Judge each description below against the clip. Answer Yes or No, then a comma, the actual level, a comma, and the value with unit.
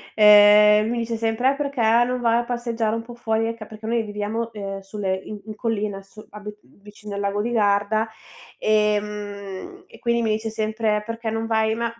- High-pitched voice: Yes, high, 215 Hz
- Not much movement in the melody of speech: Yes, narrow, 1.7 semitones